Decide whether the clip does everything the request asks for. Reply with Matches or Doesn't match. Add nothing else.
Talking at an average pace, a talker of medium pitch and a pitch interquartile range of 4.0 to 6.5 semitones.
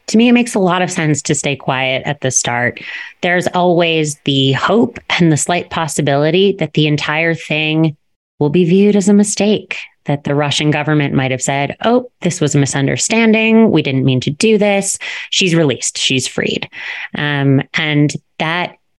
Matches